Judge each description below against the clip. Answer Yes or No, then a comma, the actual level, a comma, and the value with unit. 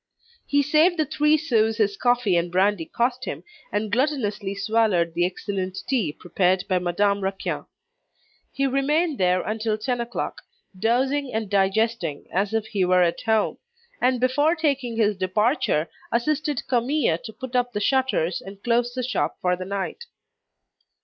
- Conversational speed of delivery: Yes, average, 155 wpm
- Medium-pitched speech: No, high, 220 Hz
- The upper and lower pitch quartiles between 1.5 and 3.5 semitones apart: No, average, 5.1 semitones